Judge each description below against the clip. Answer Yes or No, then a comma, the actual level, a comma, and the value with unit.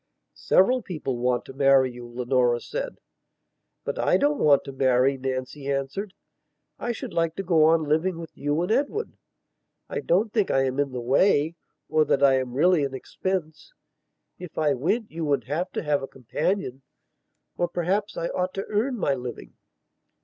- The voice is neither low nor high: Yes, medium, 150 Hz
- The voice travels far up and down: Yes, wide, 5.8 semitones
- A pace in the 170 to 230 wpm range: Yes, average, 180 wpm